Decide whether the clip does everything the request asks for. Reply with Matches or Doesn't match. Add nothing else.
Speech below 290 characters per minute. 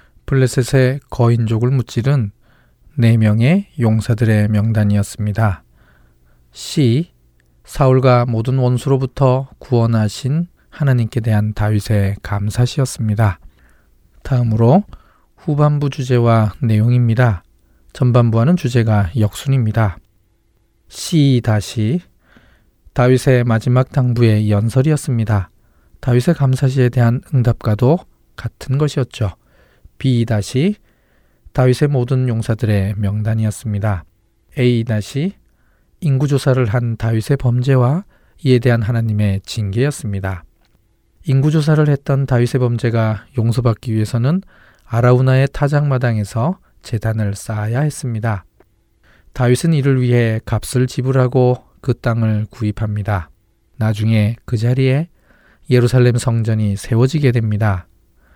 Matches